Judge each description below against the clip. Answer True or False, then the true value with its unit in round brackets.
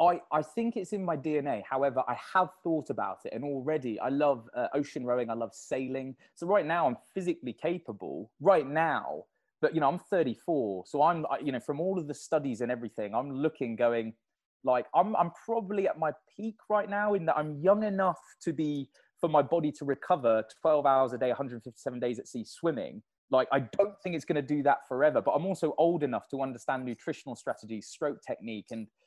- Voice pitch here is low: False (150 Hz)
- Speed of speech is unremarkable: False (215 wpm)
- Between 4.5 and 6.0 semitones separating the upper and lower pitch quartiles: True (5.1 semitones)